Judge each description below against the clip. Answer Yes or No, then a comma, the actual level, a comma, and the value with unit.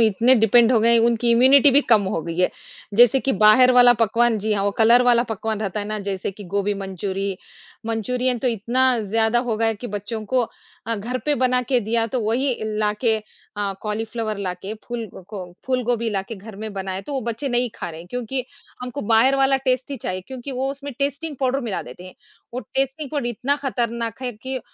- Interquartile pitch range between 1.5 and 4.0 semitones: Yes, average, 3.3 semitones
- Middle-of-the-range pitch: No, high, 230 Hz